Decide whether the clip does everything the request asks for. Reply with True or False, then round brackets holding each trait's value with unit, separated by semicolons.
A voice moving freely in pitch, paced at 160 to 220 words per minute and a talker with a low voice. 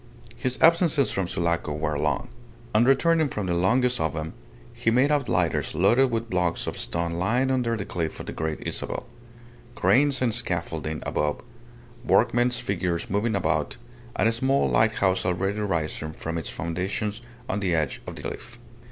True (6.5 semitones; 170 wpm; 100 Hz)